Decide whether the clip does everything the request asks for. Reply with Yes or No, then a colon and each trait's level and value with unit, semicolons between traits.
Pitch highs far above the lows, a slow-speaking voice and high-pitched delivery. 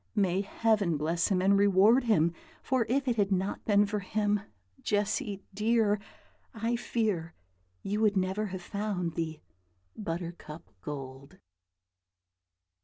No: average, 3.6 semitones; slow, 125 wpm; high, 200 Hz